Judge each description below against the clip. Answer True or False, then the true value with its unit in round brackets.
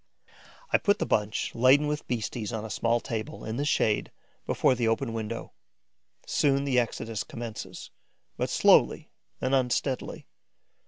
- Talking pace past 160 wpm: False (145 wpm)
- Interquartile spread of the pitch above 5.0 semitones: False (3.3 semitones)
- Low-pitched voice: True (120 Hz)